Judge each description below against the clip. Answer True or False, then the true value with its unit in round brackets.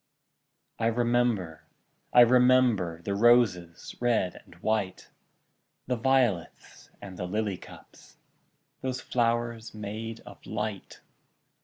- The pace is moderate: False (105 wpm)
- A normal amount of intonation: True (3.7 semitones)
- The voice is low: True (115 Hz)